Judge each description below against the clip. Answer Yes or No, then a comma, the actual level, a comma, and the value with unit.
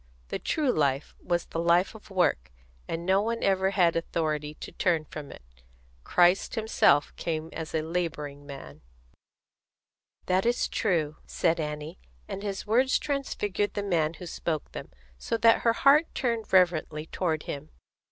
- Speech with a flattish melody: No, average, 4.7 semitones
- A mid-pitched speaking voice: Yes, medium, 175 Hz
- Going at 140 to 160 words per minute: Yes, average, 155 wpm